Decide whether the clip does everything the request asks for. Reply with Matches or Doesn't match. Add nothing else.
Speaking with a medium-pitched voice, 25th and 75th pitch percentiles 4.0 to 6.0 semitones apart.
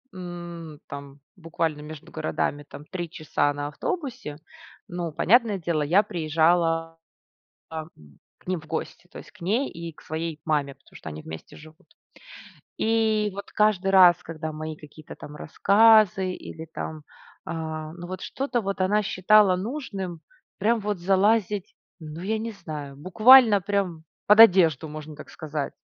Matches